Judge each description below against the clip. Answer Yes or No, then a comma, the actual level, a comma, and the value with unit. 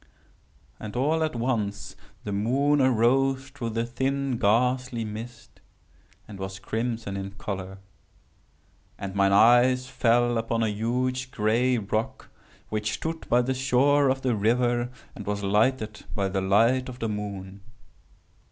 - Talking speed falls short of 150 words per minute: Yes, average, 140 wpm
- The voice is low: Yes, low, 115 Hz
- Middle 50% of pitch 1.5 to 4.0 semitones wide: Yes, average, 3.7 semitones